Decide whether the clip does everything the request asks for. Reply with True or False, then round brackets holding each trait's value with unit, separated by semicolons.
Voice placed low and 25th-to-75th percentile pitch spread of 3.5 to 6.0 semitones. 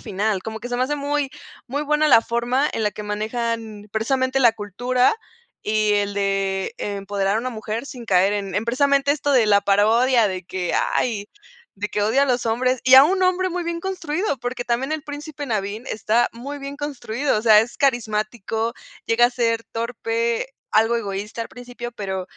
False (235 Hz; 4.0 semitones)